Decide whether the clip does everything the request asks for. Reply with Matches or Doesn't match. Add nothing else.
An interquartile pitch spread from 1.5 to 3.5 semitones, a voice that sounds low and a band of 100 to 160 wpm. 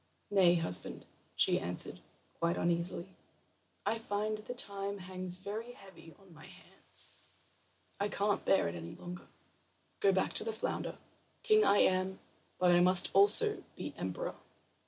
Doesn't match